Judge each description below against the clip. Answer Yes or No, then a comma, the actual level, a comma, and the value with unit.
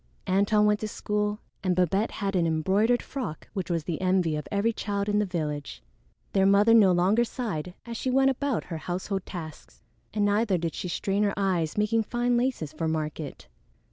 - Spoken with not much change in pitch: No, average, 3.7 semitones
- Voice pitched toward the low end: No, high, 200 Hz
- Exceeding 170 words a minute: Yes, average, 190 wpm